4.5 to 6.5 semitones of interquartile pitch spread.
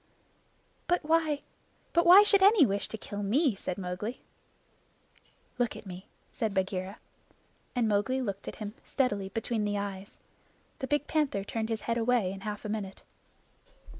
Yes: average, 5.1 semitones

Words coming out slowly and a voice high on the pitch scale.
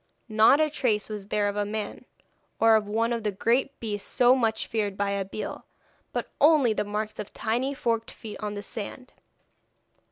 No: average, 185 wpm; high, 220 Hz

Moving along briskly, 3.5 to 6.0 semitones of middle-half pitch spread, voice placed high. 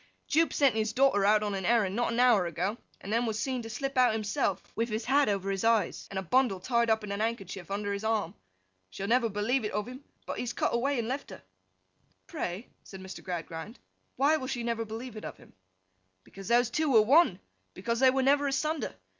Yes: fast, 230 wpm; average, 3.9 semitones; high, 225 Hz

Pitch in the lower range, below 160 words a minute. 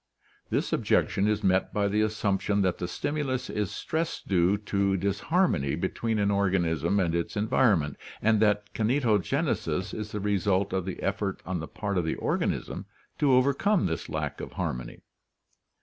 No: low, 100 Hz; average, 165 wpm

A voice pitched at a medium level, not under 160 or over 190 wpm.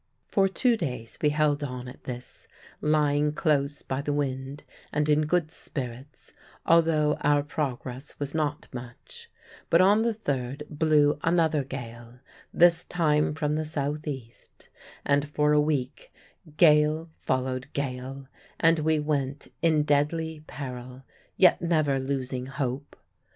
No: medium, 145 Hz; slow, 135 wpm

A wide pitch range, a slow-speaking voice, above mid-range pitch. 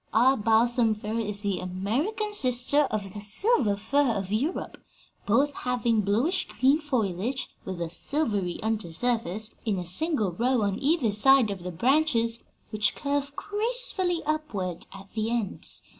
No: wide, 5.8 semitones; average, 150 wpm; high, 230 Hz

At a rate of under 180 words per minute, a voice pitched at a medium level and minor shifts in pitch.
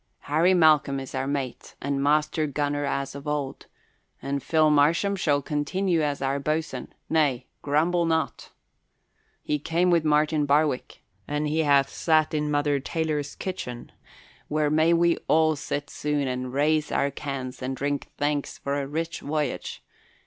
Yes: average, 155 wpm; medium, 150 Hz; narrow, 2.0 semitones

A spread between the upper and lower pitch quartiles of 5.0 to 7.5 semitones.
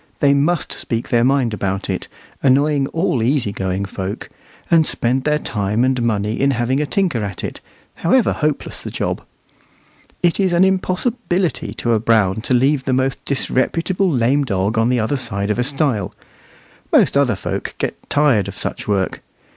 Yes: wide, 5.5 semitones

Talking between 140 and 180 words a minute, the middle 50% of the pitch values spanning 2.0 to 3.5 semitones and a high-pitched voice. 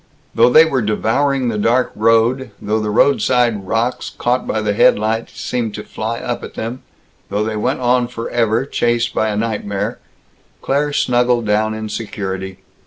No: average, 160 wpm; narrow, 2.5 semitones; low, 115 Hz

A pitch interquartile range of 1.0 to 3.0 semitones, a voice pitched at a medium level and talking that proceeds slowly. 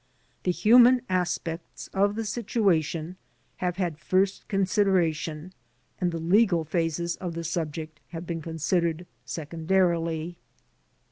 Yes: average, 2.7 semitones; medium, 170 Hz; slow, 120 wpm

